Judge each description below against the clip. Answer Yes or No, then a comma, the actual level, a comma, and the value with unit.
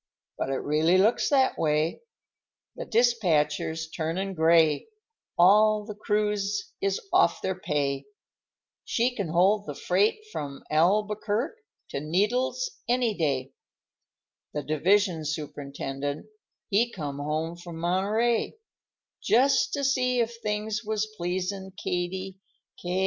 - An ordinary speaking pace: No, slow, 115 wpm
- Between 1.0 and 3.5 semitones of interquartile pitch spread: No, average, 5.3 semitones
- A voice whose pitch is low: No, high, 190 Hz